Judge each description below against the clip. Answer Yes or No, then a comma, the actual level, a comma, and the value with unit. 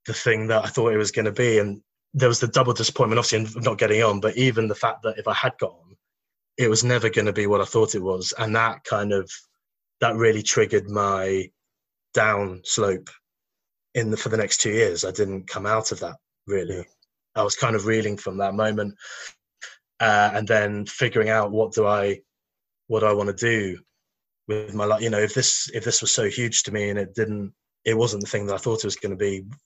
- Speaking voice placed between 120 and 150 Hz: No, low, 110 Hz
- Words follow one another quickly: Yes, fast, 235 wpm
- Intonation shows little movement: Yes, narrow, 1.9 semitones